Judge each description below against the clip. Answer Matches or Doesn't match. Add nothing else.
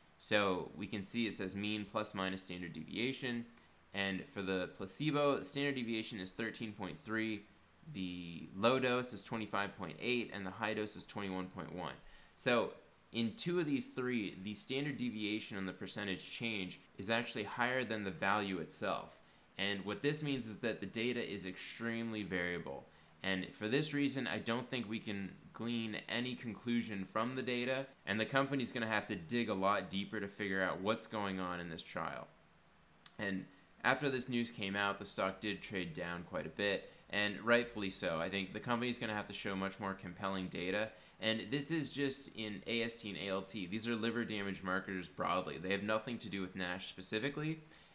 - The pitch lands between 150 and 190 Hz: Doesn't match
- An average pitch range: Matches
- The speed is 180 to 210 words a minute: Matches